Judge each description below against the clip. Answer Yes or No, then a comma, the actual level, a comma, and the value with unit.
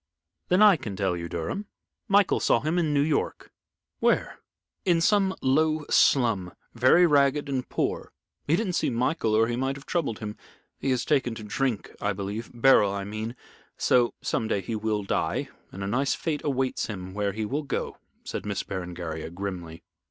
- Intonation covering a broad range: Yes, wide, 6.5 semitones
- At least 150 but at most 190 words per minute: Yes, average, 180 wpm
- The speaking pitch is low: Yes, low, 120 Hz